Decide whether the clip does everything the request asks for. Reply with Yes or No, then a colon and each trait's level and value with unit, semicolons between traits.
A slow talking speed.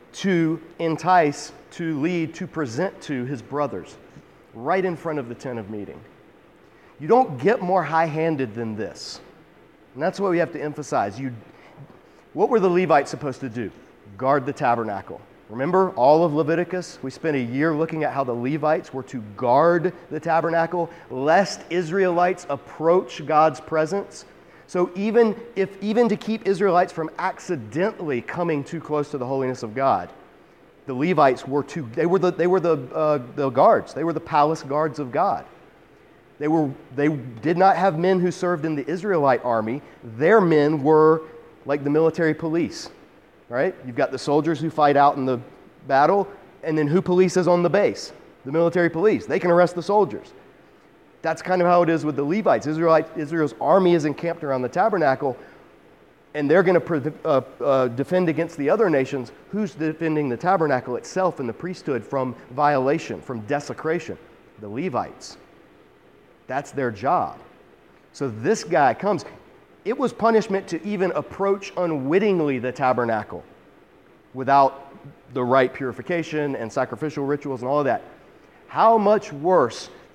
No: average, 165 wpm